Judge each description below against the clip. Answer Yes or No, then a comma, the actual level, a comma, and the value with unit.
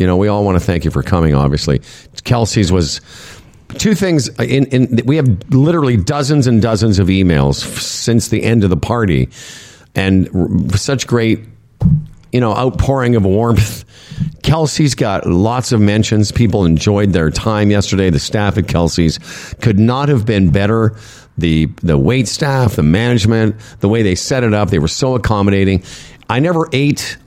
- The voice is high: No, low, 110 Hz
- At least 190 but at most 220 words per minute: No, average, 170 wpm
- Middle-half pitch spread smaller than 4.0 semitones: No, average, 4.8 semitones